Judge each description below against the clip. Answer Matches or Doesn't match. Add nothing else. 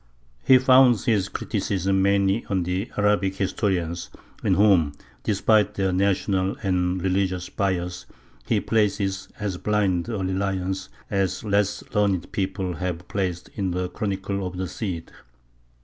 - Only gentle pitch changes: Matches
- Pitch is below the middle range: Matches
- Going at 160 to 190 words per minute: Doesn't match